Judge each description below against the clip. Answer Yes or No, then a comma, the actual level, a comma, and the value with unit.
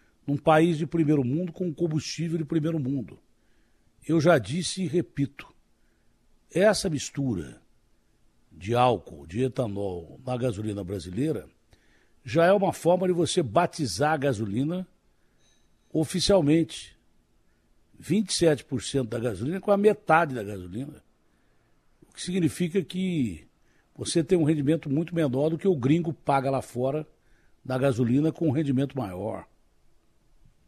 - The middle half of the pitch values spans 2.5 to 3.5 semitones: No, wide, 5.4 semitones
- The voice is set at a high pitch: No, medium, 145 Hz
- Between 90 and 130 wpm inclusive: Yes, average, 125 wpm